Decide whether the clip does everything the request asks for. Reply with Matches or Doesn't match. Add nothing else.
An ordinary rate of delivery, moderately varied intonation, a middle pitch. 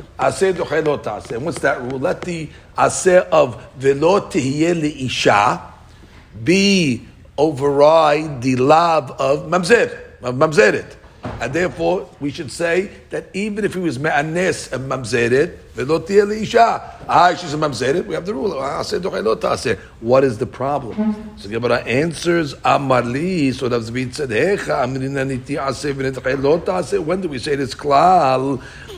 Matches